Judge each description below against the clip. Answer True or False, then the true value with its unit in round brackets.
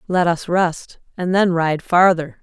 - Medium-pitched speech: True (175 Hz)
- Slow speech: False (175 wpm)